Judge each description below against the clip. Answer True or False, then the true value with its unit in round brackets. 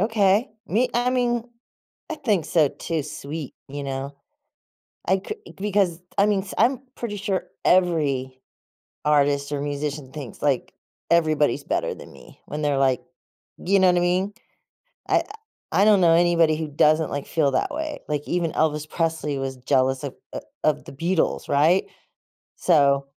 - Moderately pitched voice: True (160 Hz)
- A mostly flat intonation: False (5.1 semitones)